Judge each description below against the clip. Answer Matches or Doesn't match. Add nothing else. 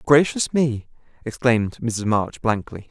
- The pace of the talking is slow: Matches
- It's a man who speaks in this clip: Matches